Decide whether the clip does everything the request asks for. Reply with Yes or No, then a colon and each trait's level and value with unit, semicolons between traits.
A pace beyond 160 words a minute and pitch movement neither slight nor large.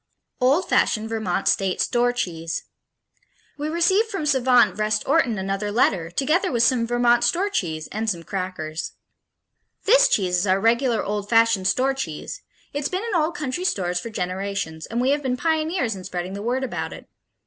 No: average, 175 wpm; wide, 6.8 semitones